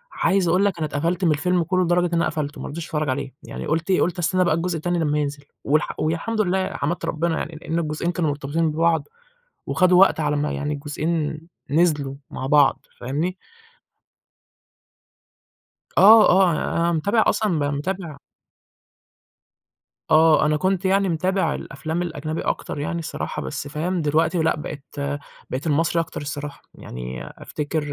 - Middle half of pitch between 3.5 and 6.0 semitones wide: No, average, 3.0 semitones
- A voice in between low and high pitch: Yes, medium, 160 Hz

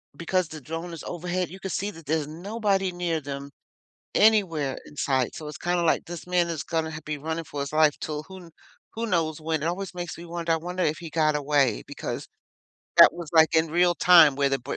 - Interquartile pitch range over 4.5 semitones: No, narrow, 2.6 semitones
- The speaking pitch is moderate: Yes, medium, 165 Hz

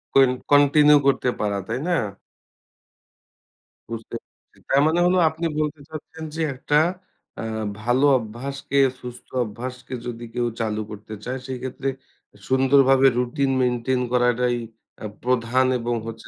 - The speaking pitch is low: Yes, low, 125 Hz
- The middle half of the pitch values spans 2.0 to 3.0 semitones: Yes, narrow, 2.5 semitones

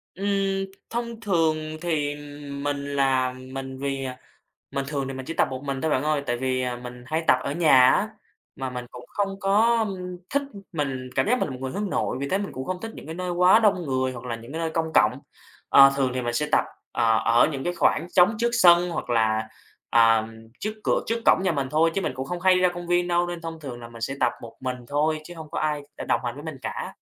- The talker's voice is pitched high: No, medium, 150 Hz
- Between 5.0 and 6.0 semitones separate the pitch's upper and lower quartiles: Yes, average, 5.3 semitones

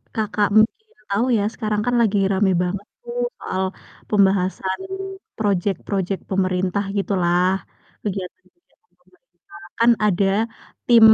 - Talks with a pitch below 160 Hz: No, high, 200 Hz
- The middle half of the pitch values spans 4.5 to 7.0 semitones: No, narrow, 2.6 semitones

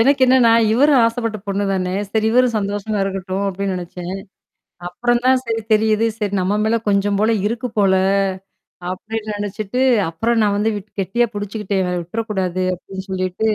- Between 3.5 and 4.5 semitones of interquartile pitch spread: No, average, 3.0 semitones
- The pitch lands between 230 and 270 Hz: No, high, 205 Hz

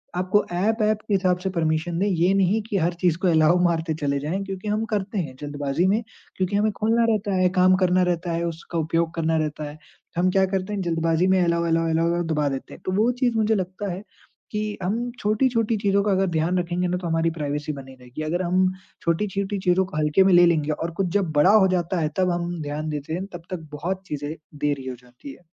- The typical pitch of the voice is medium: Yes, medium, 180 Hz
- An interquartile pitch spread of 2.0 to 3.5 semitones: Yes, average, 3.2 semitones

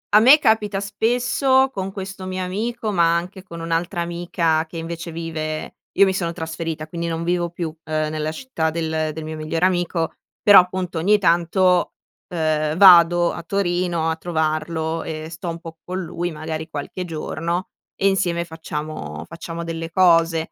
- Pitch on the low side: No, medium, 170 Hz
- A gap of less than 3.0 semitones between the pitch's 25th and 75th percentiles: Yes, narrow, 2.4 semitones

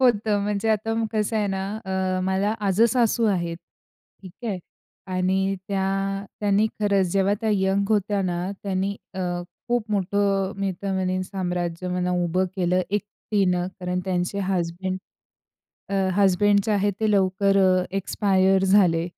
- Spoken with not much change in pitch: Yes, narrow, 1.7 semitones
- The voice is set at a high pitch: Yes, high, 195 Hz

